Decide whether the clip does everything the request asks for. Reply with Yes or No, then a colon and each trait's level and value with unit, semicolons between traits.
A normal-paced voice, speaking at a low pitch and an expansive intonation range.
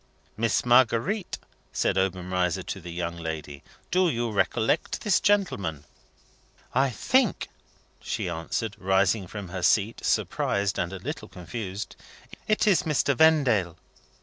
No: slow, 125 wpm; low, 100 Hz; wide, 7.1 semitones